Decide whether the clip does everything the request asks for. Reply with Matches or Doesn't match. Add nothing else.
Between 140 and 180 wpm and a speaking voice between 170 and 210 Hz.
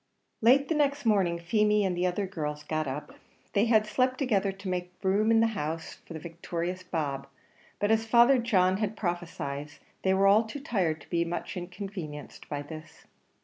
Doesn't match